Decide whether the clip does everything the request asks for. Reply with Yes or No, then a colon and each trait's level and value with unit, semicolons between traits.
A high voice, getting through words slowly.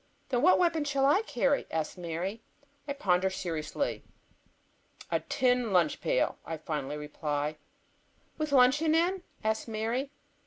Yes: high, 230 Hz; slow, 130 wpm